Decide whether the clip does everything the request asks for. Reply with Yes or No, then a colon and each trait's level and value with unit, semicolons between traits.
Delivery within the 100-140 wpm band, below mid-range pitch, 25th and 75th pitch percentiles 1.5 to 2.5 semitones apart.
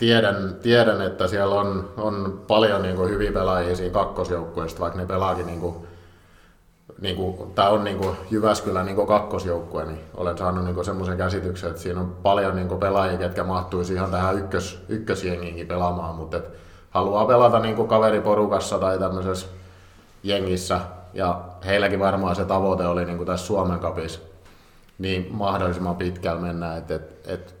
No: average, 150 wpm; very low, 95 Hz; narrow, 1.9 semitones